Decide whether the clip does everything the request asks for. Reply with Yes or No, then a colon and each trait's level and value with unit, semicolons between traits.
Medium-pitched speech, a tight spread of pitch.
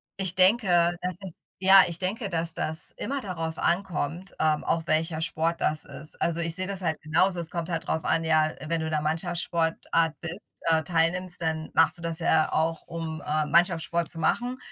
Yes: medium, 165 Hz; narrow, 2.1 semitones